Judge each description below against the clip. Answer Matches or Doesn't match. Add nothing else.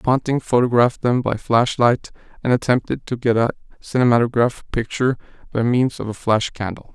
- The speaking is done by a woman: Doesn't match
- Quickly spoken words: Doesn't match